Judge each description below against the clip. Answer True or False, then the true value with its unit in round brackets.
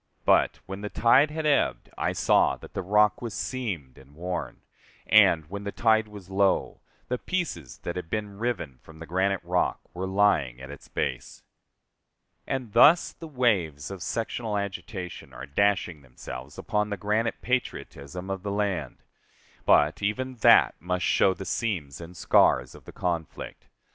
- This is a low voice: True (95 Hz)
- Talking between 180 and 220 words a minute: False (165 wpm)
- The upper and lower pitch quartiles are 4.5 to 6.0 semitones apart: True (4.9 semitones)